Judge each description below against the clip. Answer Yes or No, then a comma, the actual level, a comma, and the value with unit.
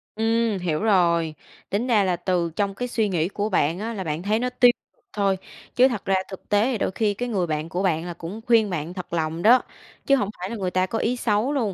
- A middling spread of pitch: Yes, average, 4.3 semitones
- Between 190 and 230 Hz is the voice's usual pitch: Yes, high, 200 Hz